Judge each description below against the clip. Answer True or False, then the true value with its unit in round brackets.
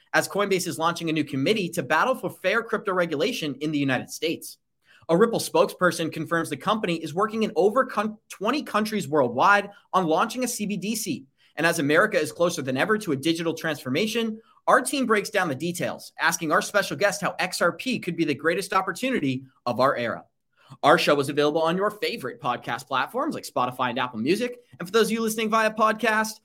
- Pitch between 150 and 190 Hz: True (185 Hz)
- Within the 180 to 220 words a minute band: True (195 wpm)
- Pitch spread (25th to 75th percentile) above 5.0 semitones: True (5.5 semitones)